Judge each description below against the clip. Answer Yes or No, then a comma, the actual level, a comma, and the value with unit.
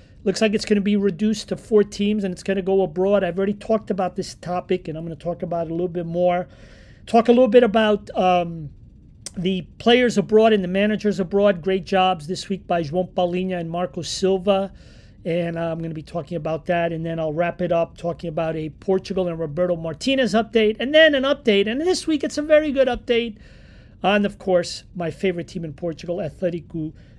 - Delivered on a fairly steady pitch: No, average, 3.6 semitones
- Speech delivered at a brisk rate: Yes, fast, 220 wpm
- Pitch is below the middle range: No, medium, 185 Hz